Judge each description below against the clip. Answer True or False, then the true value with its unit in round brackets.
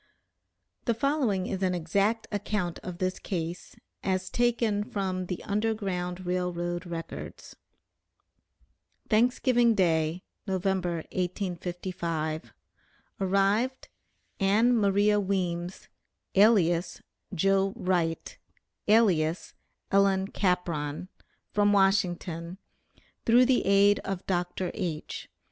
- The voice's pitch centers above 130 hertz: True (190 Hz)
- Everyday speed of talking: False (90 wpm)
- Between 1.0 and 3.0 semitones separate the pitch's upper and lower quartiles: True (2.7 semitones)